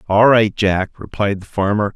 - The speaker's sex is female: No, male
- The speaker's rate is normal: Yes, average, 185 wpm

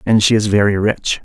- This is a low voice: Yes, low, 105 Hz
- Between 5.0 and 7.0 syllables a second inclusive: Yes, 5.4 syllables/s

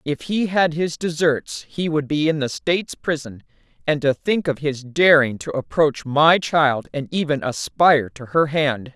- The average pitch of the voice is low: No, medium, 150 Hz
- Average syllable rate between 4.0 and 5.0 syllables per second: Yes, 4.3 syllables/s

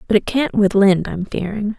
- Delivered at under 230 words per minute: No, fast, 235 wpm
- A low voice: No, high, 205 Hz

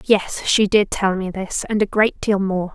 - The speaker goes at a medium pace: No, fast, 240 wpm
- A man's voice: No, female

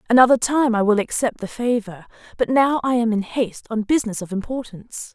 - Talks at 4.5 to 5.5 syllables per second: No, 5.9 syllables/s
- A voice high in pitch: Yes, high, 230 Hz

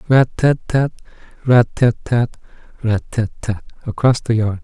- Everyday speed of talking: No, slow, 115 wpm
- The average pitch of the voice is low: Yes, low, 120 Hz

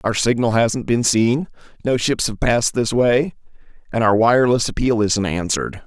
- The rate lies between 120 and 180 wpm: Yes, average, 175 wpm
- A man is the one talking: Yes, male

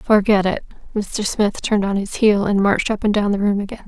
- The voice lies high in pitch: Yes, high, 205 Hz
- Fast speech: Yes, fast, 250 wpm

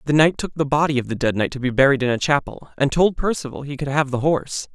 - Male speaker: Yes, male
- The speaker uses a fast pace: Yes, fast, 290 wpm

